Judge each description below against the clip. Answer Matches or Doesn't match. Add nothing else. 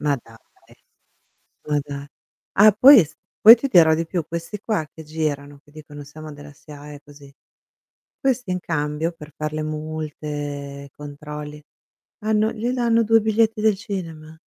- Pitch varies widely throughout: Matches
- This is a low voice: Doesn't match